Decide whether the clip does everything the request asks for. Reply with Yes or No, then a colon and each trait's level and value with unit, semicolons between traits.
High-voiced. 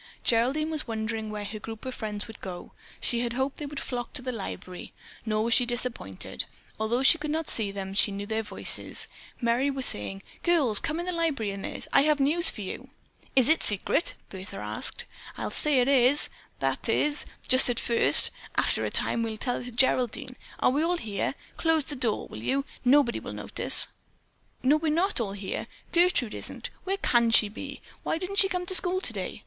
Yes: very high, 250 Hz